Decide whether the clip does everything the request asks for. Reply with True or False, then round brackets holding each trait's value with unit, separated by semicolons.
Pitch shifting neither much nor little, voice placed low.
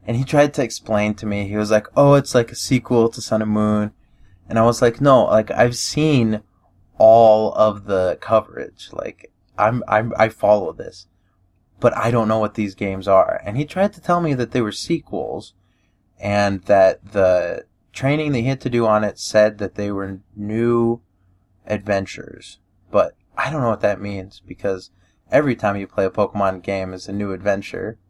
True (3.3 semitones; 105 Hz)